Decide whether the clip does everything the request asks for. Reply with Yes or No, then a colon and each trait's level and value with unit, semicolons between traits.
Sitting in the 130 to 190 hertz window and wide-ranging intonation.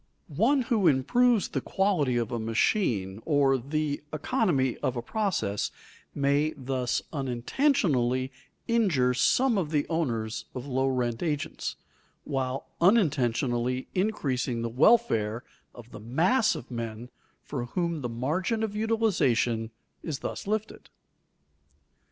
Yes: medium, 140 Hz; wide, 7.9 semitones